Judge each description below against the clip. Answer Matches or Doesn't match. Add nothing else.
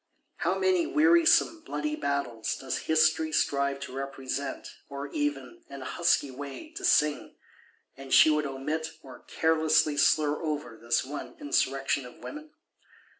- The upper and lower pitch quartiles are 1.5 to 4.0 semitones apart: Matches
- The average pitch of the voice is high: Doesn't match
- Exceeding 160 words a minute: Doesn't match